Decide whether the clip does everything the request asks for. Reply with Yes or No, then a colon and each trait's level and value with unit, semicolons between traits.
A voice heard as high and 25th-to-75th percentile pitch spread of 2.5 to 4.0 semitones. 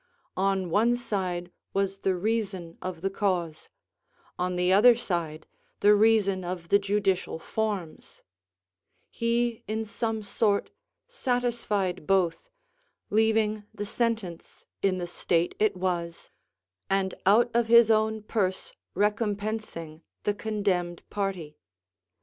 Yes: high, 200 Hz; average, 3.3 semitones